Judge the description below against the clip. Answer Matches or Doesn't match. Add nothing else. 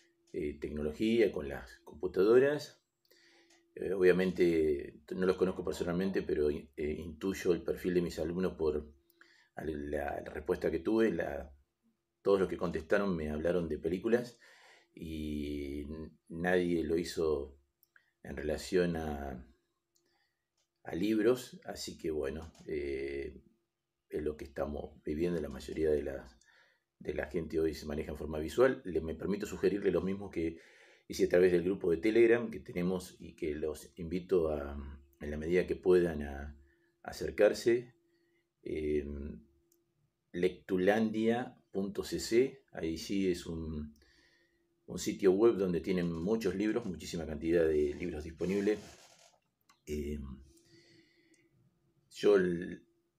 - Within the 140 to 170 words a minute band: Doesn't match